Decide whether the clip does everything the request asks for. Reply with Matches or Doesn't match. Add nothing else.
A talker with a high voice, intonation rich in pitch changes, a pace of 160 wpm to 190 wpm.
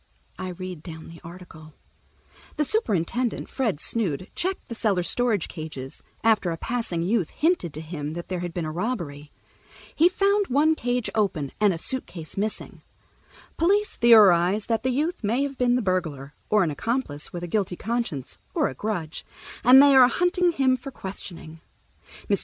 Matches